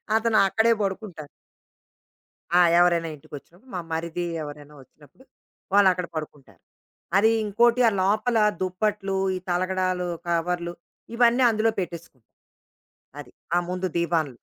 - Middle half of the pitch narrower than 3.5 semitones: No, average, 4.2 semitones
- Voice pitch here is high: No, medium, 180 Hz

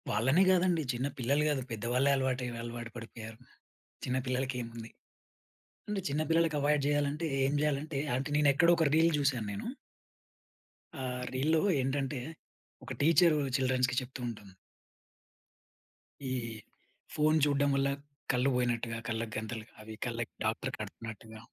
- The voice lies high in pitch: No, low, 130 Hz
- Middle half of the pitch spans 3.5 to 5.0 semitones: Yes, average, 3.9 semitones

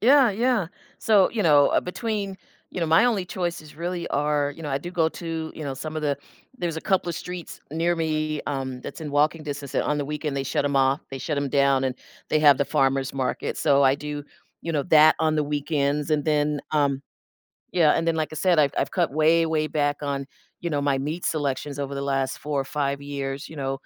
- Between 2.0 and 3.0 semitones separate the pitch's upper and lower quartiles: Yes, average, 2.7 semitones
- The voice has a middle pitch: Yes, medium, 150 Hz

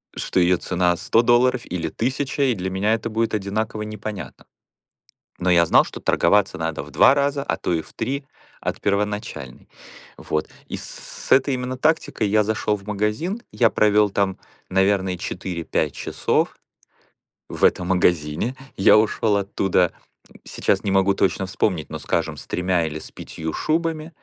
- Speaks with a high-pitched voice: No, low, 100 Hz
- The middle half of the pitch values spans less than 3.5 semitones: No, average, 4.1 semitones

